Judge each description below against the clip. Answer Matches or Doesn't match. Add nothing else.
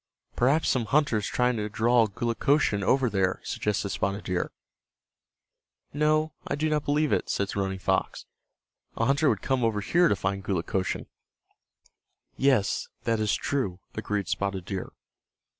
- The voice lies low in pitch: Matches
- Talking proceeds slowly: Doesn't match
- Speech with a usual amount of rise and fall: Doesn't match